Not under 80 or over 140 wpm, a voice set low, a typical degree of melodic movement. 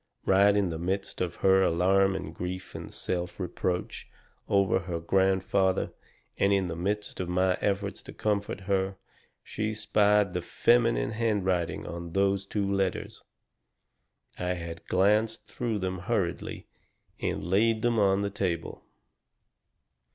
No: slow, 135 wpm; very low, 95 Hz; narrow, 2.1 semitones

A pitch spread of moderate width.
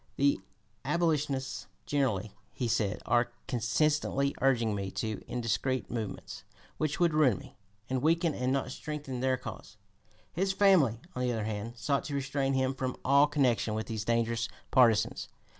Yes: average, 3.8 semitones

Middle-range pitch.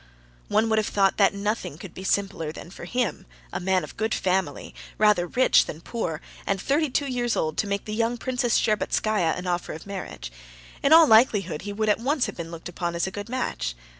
No: high, 200 Hz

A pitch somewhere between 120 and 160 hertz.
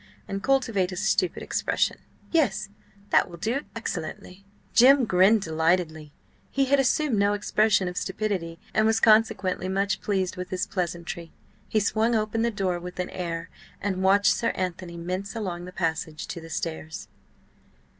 No: high, 190 Hz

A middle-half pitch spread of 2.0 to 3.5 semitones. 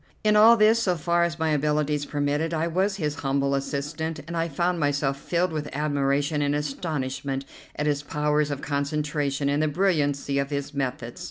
Yes: narrow, 2.6 semitones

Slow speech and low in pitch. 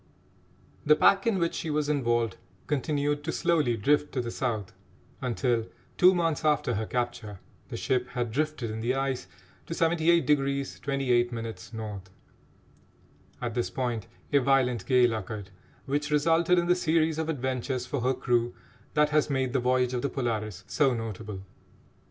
No: average, 155 wpm; low, 130 Hz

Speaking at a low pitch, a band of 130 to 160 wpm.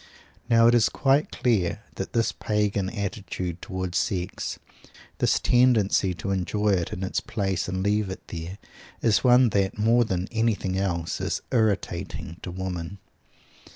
Yes: low, 100 Hz; average, 150 wpm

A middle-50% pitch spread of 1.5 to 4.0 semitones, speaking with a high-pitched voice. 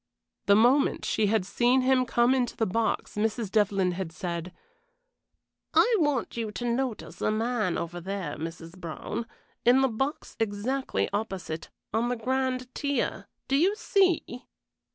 No: average, 5.0 semitones; high, 230 Hz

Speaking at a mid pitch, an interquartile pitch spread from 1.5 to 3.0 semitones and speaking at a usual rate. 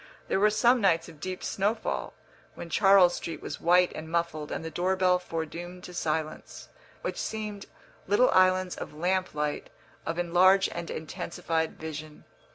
Yes: medium, 175 Hz; average, 2.7 semitones; average, 160 wpm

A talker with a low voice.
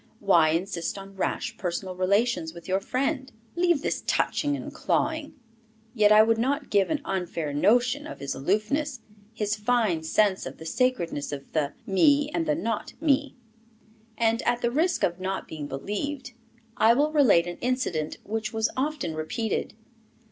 No: high, 220 Hz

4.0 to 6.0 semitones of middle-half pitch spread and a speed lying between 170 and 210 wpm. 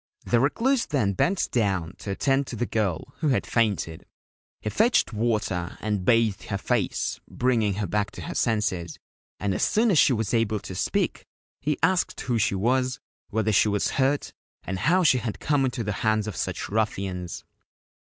Yes: average, 4.7 semitones; average, 180 wpm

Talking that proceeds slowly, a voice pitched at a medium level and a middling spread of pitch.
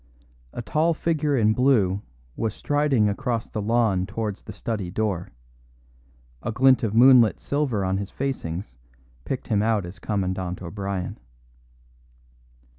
No: slow, 130 wpm; low, 110 Hz; average, 4.6 semitones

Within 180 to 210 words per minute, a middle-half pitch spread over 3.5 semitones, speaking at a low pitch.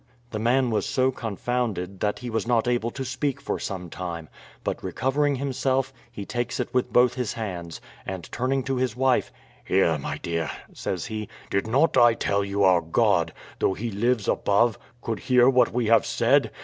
Yes: average, 190 wpm; average, 4.4 semitones; low, 115 Hz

